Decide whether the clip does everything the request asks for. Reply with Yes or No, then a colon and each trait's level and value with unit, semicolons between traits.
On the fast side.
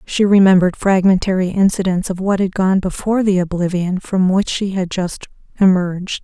No: average, 165 wpm